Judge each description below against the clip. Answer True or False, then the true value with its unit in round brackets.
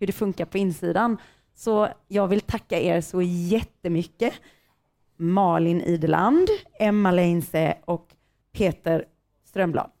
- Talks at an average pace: False (115 wpm)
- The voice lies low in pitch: False (180 Hz)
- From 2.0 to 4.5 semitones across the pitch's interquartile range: True (3.7 semitones)